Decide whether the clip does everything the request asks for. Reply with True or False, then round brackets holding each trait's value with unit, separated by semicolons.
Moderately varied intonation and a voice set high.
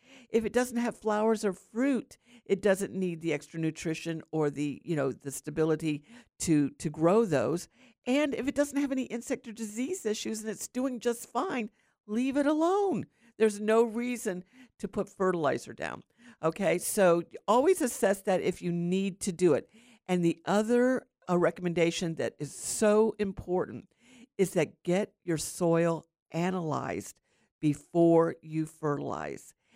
False (6.1 semitones; 195 Hz)